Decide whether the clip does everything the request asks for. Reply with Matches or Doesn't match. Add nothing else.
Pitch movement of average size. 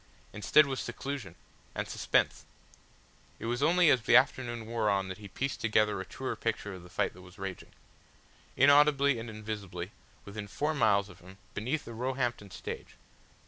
Matches